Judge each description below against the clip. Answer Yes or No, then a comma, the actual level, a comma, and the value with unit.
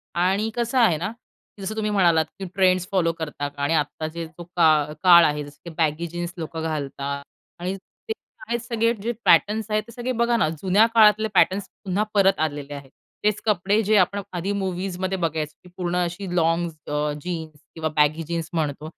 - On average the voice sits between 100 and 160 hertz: No, medium, 175 Hz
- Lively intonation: No, average, 4.3 semitones